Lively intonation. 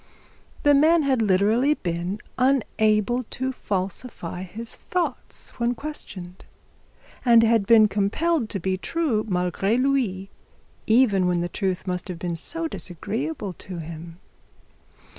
Yes: wide, 5.8 semitones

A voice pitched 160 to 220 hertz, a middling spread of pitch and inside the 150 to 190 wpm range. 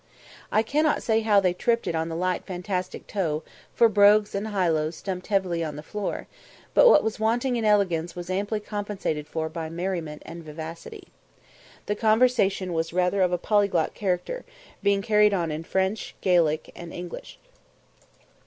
Yes: medium, 185 Hz; average, 3.9 semitones; average, 165 wpm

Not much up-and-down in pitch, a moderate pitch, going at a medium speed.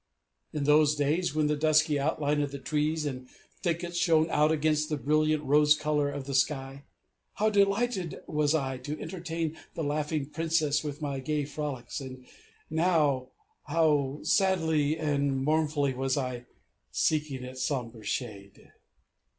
Yes: narrow, 2.2 semitones; medium, 150 Hz; average, 145 wpm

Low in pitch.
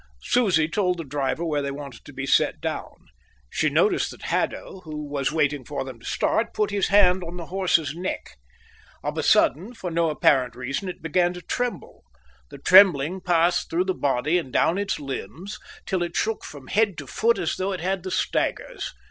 No: medium, 170 Hz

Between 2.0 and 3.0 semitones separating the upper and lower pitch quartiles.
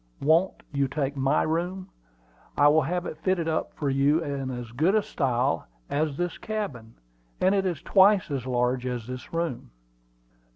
No: average, 5.1 semitones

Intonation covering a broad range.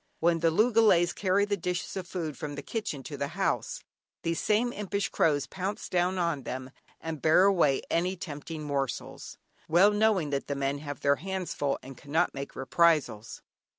No: average, 4.9 semitones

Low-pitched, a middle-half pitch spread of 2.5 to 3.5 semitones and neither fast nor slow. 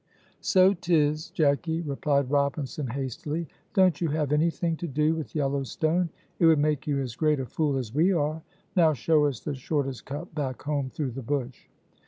No: medium, 150 Hz; average, 2.8 semitones; average, 185 wpm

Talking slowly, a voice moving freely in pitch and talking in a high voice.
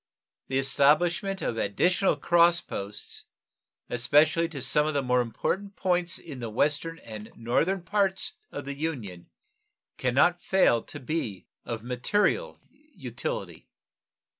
No: slow, 125 wpm; wide, 6.5 semitones; medium, 150 Hz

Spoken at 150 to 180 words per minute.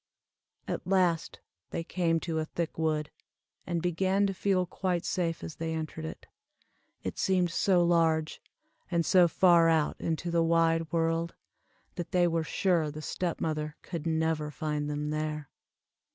Yes: average, 155 wpm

